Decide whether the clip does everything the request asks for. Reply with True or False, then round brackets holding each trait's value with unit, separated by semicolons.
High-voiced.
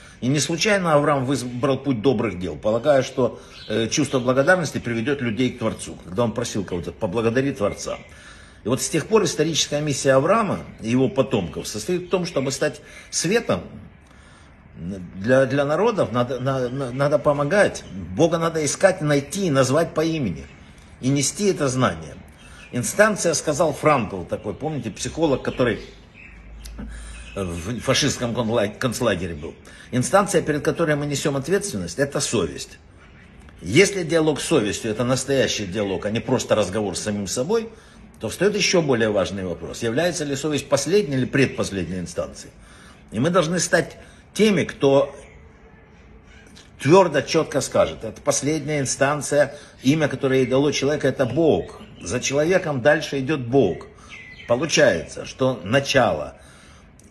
False (135 Hz)